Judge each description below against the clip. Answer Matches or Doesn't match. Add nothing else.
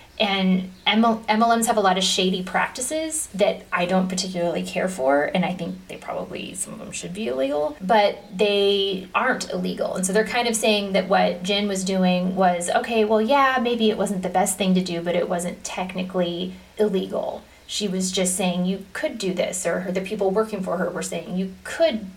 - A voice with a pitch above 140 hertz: Matches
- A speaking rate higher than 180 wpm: Matches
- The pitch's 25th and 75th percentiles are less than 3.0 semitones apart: Matches